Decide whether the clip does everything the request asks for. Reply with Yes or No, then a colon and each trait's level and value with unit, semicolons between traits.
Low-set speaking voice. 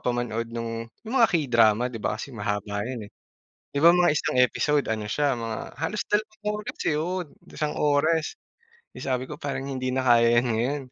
Yes: low, 130 Hz